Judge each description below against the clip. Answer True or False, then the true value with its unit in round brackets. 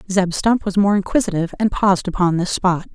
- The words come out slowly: False (205 wpm)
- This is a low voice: False (190 Hz)